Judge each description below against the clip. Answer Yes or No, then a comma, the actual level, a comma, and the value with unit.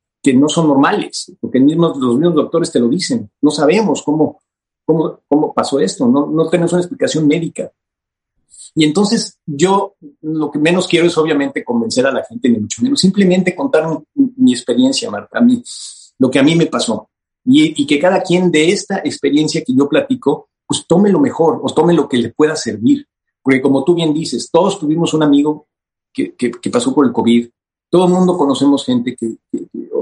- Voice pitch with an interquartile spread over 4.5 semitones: Yes, average, 5.1 semitones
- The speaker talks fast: Yes, fast, 200 wpm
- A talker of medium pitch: Yes, medium, 160 Hz